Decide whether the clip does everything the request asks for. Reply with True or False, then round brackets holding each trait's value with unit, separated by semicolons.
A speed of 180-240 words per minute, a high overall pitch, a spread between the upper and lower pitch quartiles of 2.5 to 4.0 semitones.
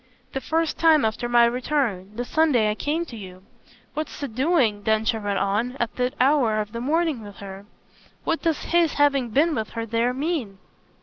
False (190 wpm; 245 Hz; 5.6 semitones)